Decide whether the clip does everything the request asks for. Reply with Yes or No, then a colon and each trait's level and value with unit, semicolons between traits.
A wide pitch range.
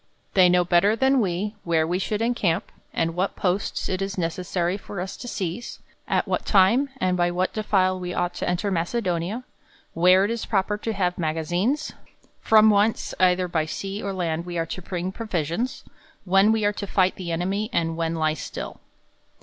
No: average, 2.9 semitones